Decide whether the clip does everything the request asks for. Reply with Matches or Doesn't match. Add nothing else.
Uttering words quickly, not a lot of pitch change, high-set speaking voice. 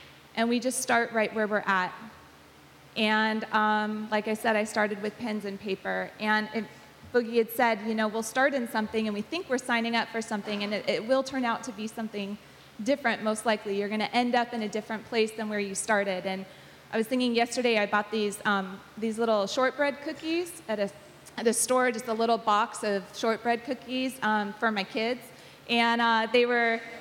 Matches